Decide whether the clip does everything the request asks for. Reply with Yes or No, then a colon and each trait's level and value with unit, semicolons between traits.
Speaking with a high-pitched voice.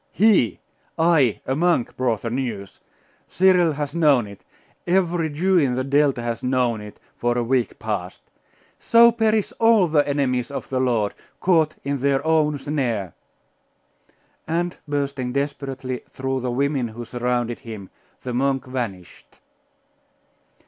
No: low, 135 Hz